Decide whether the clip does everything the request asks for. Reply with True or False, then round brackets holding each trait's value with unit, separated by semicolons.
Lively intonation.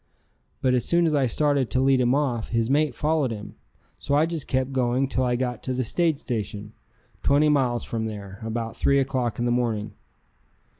False (3.2 semitones)